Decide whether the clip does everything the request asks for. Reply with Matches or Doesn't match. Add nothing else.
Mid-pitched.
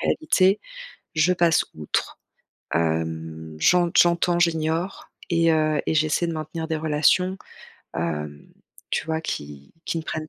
Matches